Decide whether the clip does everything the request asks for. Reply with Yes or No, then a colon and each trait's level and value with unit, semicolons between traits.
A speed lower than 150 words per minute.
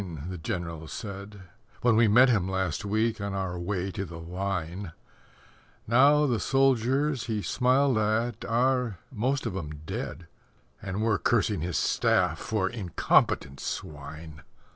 Yes: average, 140 wpm